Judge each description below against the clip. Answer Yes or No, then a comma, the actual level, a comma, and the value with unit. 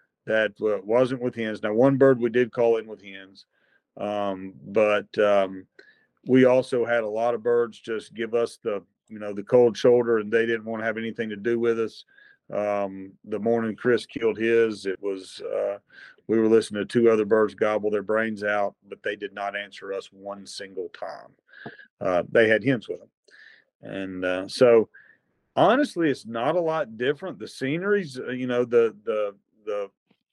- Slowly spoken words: No, average, 185 wpm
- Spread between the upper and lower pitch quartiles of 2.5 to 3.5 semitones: Yes, average, 3.0 semitones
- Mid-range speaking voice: No, low, 115 Hz